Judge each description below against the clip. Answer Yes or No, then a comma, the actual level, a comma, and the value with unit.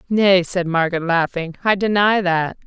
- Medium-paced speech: Yes, average, 155 wpm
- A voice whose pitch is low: No, medium, 185 Hz